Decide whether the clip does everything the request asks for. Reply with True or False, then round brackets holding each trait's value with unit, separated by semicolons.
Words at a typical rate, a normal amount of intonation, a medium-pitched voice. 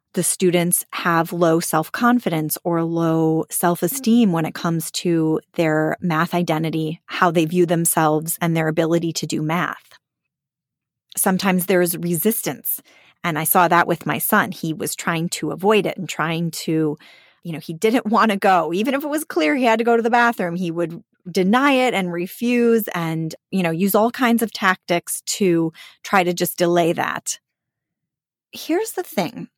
True (180 wpm; 4.1 semitones; 175 Hz)